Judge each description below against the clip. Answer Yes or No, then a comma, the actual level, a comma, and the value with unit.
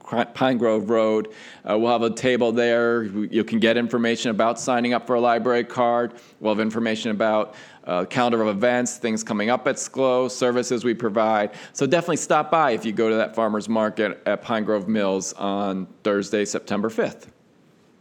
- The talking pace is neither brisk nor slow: Yes, average, 185 wpm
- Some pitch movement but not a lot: No, narrow, 2.1 semitones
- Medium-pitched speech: No, low, 115 Hz